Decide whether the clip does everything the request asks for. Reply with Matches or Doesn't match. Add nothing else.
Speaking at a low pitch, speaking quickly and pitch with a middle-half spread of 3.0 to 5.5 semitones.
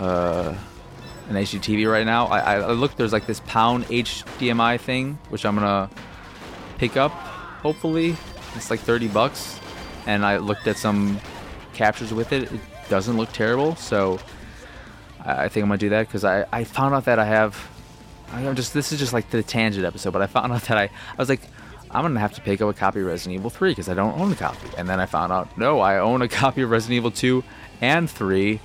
Matches